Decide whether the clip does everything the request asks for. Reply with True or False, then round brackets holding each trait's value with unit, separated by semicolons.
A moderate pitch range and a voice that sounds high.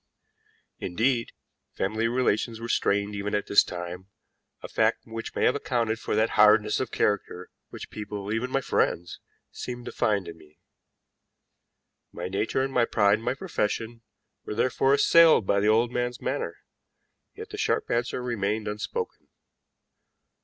False (3.1 semitones; 110 Hz)